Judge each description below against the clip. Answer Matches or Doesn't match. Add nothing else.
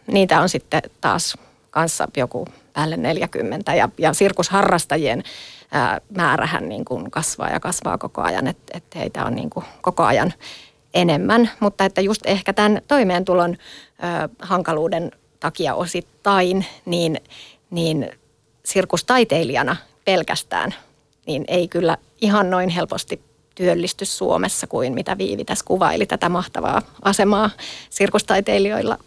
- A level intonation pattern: Doesn't match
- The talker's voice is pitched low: Doesn't match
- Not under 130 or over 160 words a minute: Doesn't match